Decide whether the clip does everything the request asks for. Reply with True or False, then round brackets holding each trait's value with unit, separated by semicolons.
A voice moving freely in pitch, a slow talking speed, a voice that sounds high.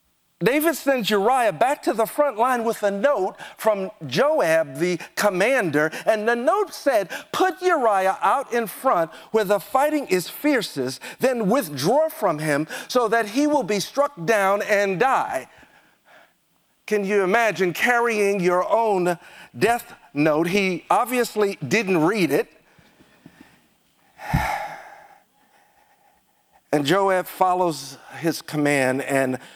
True (7.6 semitones; 125 wpm; 210 Hz)